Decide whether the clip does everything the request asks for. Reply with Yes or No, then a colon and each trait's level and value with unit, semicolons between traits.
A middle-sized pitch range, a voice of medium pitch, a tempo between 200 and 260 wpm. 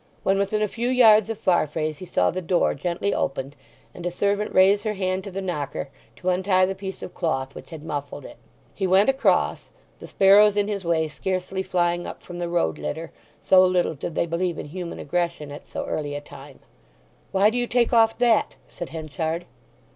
Yes: average, 3.8 semitones; medium, 180 Hz; fast, 205 wpm